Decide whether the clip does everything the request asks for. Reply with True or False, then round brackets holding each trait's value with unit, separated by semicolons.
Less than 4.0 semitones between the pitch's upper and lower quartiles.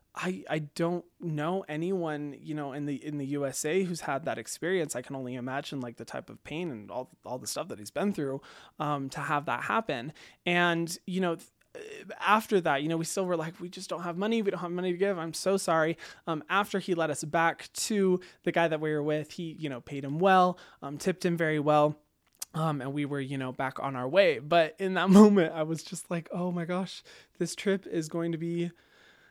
True (3.5 semitones)